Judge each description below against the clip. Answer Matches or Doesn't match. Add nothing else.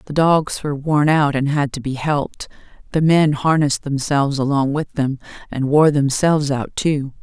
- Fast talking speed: Doesn't match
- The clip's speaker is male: Doesn't match